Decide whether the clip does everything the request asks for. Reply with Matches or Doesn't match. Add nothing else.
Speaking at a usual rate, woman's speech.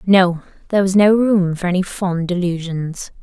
Matches